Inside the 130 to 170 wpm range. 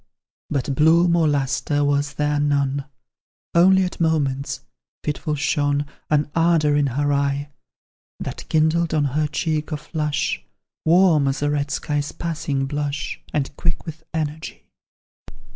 Yes: slow, 135 wpm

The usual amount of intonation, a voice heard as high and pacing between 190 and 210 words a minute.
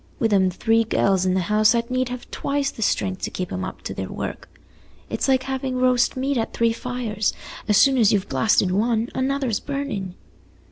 Yes: average, 4.3 semitones; high, 230 Hz; average, 200 wpm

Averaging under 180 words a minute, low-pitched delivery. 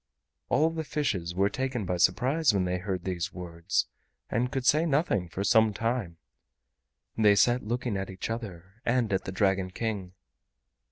Yes: average, 165 wpm; low, 105 Hz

